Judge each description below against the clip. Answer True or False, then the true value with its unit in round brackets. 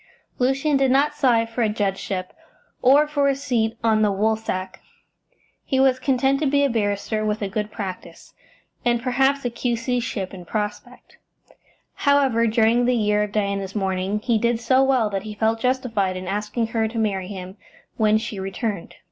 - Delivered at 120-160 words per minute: False (175 wpm)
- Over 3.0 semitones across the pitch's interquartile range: True (3.7 semitones)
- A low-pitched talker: False (225 Hz)